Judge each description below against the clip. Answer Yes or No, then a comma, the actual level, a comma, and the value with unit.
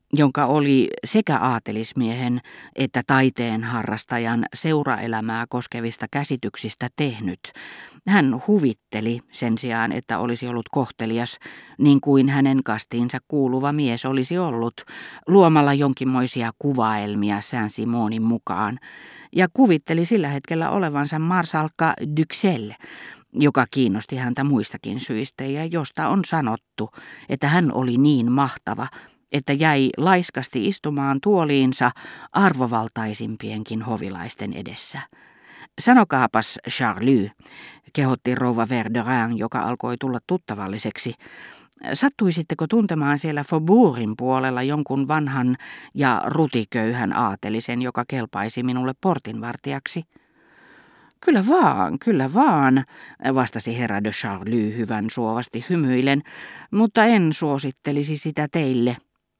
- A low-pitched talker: Yes, low, 130 Hz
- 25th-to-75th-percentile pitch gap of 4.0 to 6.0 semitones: Yes, average, 4.3 semitones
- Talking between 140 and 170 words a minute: No, average, 100 wpm